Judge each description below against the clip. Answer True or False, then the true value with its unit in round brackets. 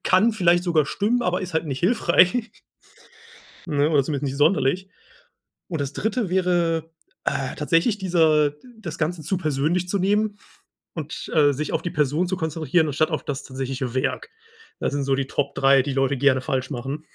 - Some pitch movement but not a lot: True (4.5 semitones)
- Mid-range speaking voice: True (155 Hz)